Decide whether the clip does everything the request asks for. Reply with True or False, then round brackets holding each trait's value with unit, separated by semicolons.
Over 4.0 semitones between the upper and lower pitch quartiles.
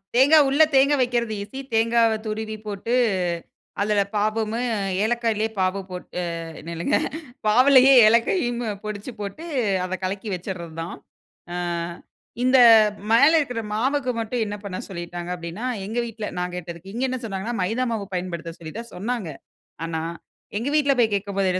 True (4.4 semitones)